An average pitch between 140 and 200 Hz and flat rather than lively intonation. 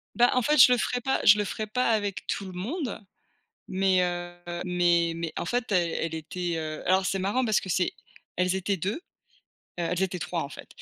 No: medium, 185 Hz; average, 3.4 semitones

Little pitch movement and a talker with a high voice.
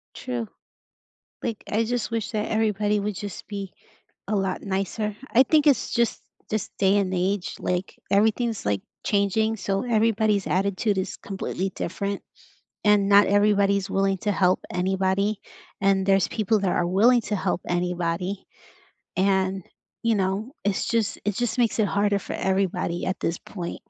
Yes: narrow, 2.2 semitones; high, 200 Hz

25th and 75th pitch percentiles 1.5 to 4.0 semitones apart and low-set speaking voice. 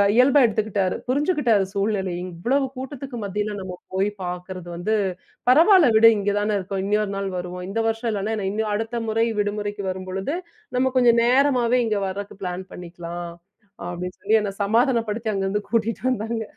No: average, 3.5 semitones; high, 210 Hz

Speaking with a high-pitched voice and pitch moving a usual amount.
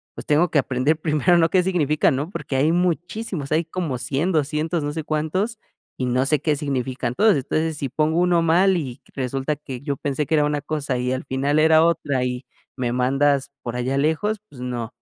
No: medium, 150 Hz; average, 3.6 semitones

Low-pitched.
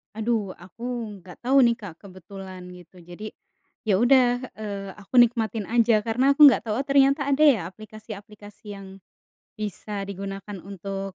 No: high, 210 Hz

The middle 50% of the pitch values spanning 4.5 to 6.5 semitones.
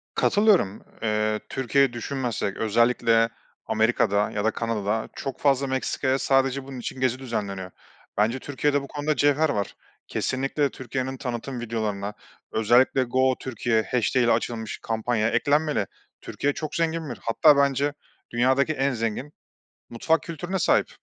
No: average, 3.7 semitones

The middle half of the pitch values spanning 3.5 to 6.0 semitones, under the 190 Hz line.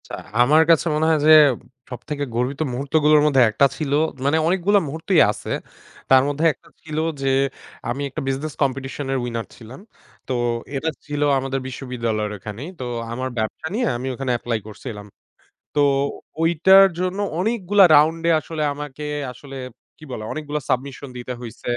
Yes: average, 3.8 semitones; medium, 140 Hz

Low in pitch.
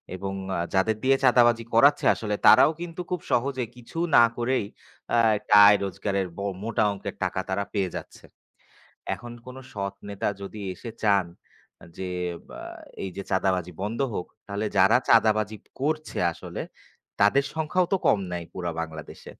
Yes: low, 105 Hz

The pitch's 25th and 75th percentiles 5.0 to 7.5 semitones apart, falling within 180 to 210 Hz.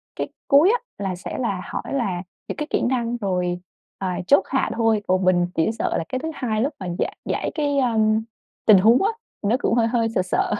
No: wide, 5.6 semitones; high, 225 Hz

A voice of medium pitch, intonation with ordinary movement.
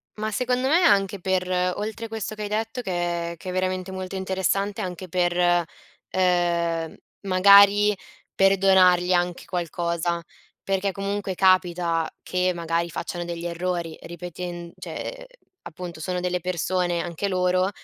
No: medium, 180 Hz; narrow, 2.1 semitones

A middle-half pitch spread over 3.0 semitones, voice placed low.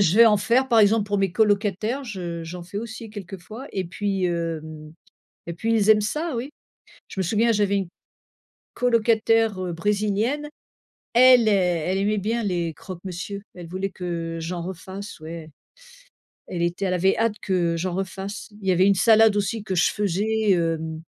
No: average, 3.7 semitones; high, 195 Hz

